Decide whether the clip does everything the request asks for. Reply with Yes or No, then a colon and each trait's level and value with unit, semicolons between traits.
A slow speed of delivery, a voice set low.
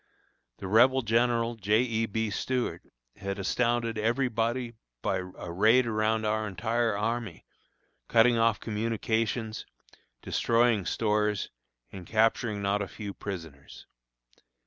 Yes: slow, 120 wpm; low, 110 Hz